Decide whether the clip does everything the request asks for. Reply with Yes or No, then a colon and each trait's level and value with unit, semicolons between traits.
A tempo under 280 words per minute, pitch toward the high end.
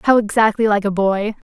Yes: average, 200 wpm; high, 210 Hz